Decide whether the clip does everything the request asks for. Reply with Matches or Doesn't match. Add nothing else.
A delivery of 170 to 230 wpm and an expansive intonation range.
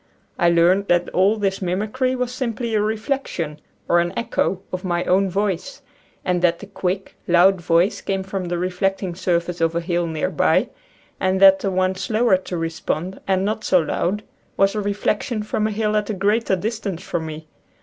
Doesn't match